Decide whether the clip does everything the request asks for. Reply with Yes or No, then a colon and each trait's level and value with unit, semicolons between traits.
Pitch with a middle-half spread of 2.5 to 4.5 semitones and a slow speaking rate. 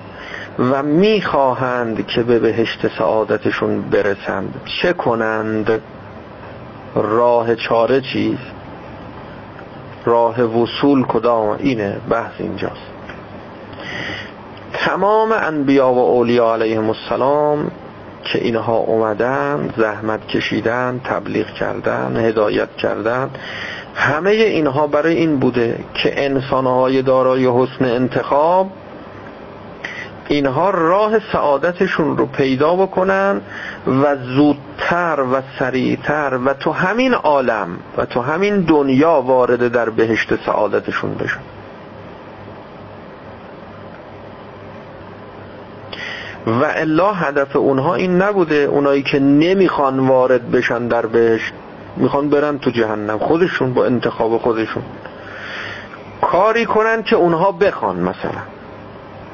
No: average, 4.9 semitones; slow, 95 wpm